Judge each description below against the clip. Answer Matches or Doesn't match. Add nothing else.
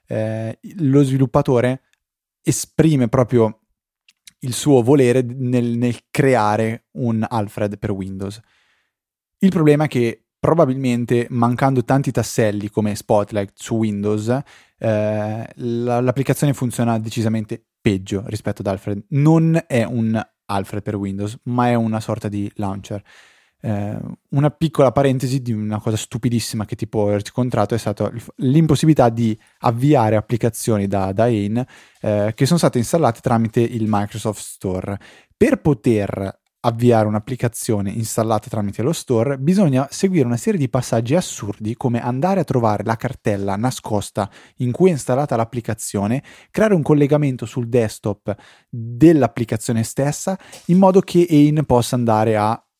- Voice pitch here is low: Matches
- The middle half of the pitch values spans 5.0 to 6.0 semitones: Doesn't match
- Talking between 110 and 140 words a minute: Matches